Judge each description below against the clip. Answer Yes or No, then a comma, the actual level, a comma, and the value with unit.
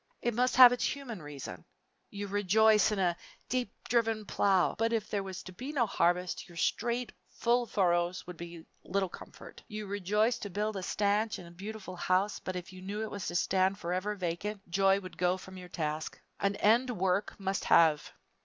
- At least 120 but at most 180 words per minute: No, average, 190 wpm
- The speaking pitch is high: Yes, high, 195 Hz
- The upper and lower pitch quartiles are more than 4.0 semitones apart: No, average, 3.2 semitones